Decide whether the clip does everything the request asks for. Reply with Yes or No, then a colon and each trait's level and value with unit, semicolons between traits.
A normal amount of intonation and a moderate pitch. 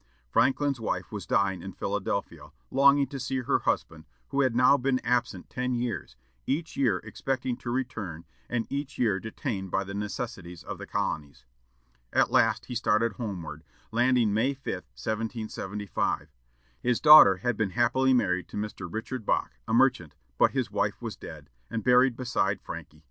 No: average, 4.8 semitones; low, 115 Hz